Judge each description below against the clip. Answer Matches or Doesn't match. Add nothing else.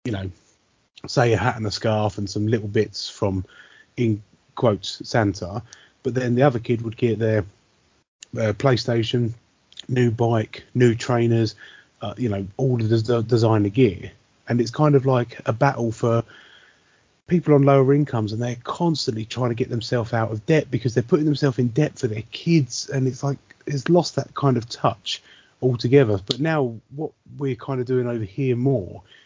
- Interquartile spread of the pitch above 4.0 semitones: Doesn't match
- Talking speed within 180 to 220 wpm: Matches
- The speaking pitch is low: Matches